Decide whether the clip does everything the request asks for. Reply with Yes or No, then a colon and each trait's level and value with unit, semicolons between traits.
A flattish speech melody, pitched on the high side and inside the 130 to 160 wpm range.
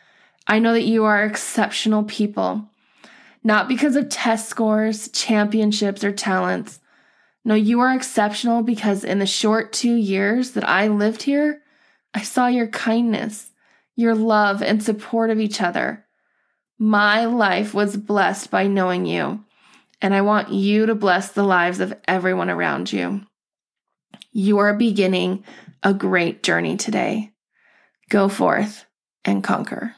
Yes: narrow, 2.0 semitones; high, 215 Hz; average, 140 wpm